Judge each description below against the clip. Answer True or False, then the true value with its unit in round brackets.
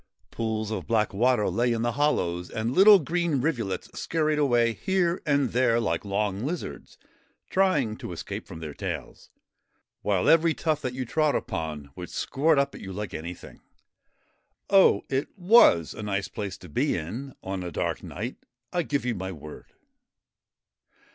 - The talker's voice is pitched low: True (120 Hz)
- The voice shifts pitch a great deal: True (7.4 semitones)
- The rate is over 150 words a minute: True (165 wpm)